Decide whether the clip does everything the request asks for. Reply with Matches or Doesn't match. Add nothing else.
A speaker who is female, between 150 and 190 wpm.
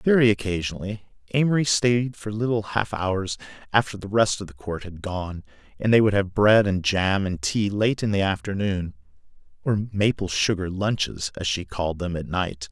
Doesn't match